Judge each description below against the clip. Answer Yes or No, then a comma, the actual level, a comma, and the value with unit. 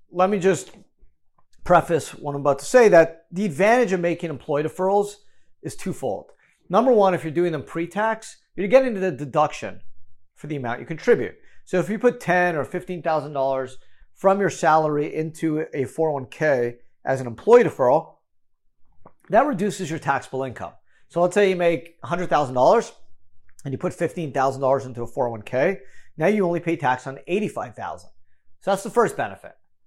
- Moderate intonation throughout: No, wide, 6.1 semitones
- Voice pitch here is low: No, medium, 160 Hz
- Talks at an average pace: Yes, average, 165 wpm